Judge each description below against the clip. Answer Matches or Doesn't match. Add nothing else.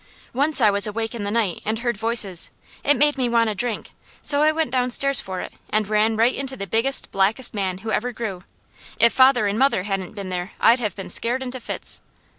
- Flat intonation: Doesn't match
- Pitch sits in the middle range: Doesn't match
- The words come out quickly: Matches